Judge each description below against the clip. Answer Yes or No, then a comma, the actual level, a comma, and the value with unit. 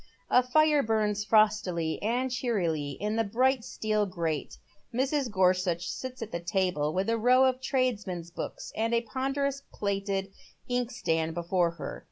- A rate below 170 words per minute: Yes, average, 155 wpm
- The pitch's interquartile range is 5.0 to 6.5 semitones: Yes, wide, 5.6 semitones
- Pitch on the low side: No, high, 210 Hz